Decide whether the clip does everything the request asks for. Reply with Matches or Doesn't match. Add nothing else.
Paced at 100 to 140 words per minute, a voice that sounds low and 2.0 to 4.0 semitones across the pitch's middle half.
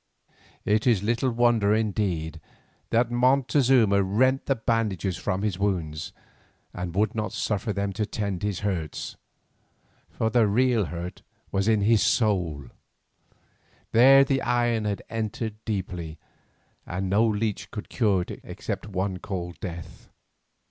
Matches